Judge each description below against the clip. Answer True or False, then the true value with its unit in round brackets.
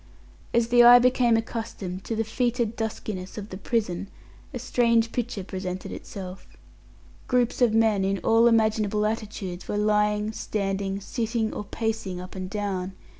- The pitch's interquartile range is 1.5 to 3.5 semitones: True (2.9 semitones)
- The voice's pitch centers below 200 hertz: False (215 Hz)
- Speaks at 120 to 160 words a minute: True (150 wpm)